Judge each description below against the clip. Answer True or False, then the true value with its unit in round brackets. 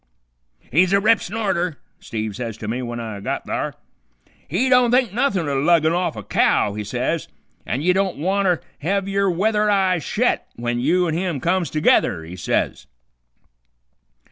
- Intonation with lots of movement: True (8.2 semitones)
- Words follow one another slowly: False (170 wpm)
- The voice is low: False (170 Hz)